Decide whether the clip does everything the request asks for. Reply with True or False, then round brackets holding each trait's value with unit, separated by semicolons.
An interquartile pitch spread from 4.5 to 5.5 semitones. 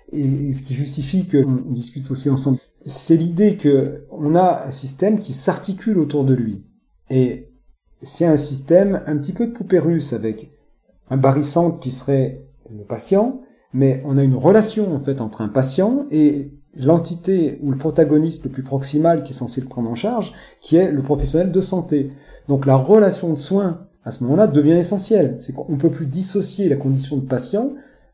True (5.0 semitones)